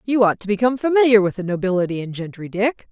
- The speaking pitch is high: Yes, high, 210 Hz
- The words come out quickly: Yes, fast, 225 wpm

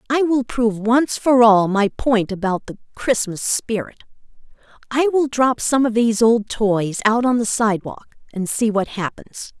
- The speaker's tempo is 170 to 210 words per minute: Yes, average, 175 wpm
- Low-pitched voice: No, high, 225 Hz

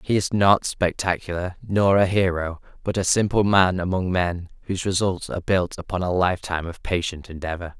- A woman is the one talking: No, male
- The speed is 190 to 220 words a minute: No, average, 175 wpm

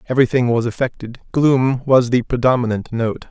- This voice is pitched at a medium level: No, low, 125 Hz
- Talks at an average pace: Yes, average, 145 wpm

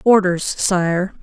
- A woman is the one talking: Yes, female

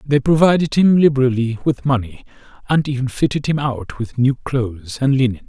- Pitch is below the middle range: Yes, low, 130 Hz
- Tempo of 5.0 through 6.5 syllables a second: Yes, 5.4 syllables/s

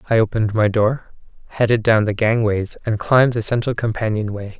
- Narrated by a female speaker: No, male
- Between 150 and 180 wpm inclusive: Yes, average, 170 wpm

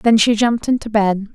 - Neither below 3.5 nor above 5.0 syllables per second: No, 5.5 syllables/s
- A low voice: No, high, 220 Hz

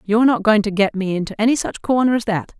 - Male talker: No, female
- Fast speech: Yes, fast, 275 wpm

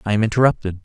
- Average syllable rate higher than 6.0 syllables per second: Yes, 8.2 syllables/s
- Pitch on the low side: Yes, low, 110 Hz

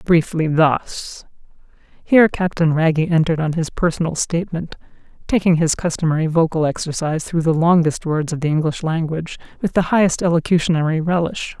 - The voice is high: No, medium, 165 Hz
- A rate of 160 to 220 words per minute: No, average, 145 wpm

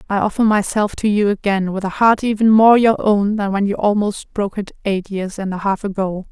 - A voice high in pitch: Yes, high, 205 Hz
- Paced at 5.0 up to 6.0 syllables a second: Yes, 5.4 syllables/s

